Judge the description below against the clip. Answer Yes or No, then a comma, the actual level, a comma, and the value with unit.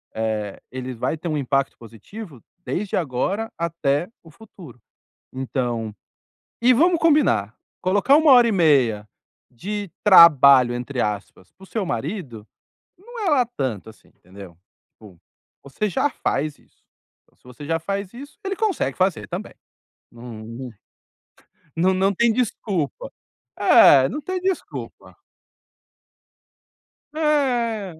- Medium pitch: Yes, medium, 165 Hz